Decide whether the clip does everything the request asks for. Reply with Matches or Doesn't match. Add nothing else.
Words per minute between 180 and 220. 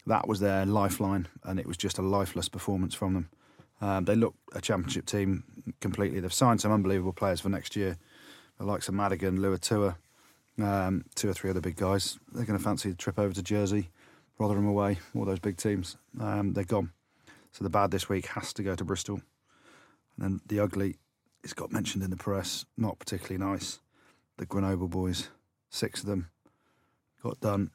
Matches